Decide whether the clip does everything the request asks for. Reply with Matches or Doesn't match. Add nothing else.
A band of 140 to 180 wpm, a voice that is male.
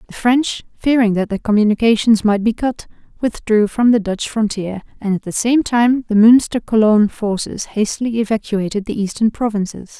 Doesn't match